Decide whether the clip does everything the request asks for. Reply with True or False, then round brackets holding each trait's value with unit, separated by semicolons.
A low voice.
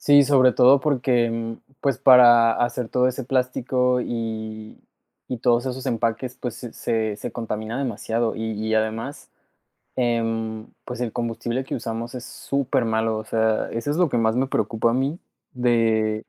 True (120 Hz)